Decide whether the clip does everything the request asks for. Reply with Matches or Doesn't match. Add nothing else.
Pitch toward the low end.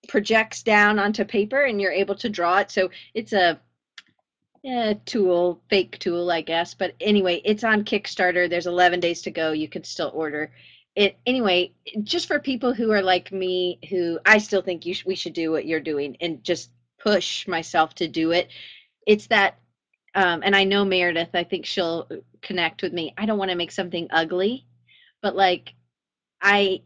Doesn't match